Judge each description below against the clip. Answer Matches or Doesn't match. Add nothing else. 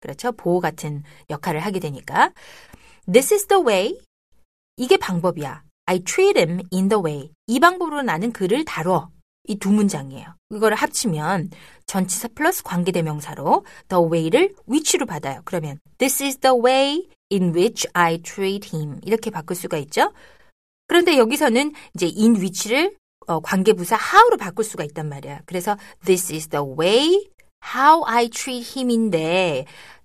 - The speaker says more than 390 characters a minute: Matches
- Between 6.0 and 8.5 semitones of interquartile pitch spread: Matches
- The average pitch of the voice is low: Doesn't match